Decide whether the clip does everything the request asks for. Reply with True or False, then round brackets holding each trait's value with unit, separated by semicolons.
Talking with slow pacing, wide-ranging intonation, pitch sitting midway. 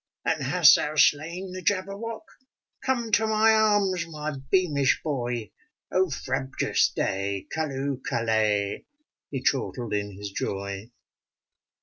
True (120 wpm; 8.9 semitones; 145 Hz)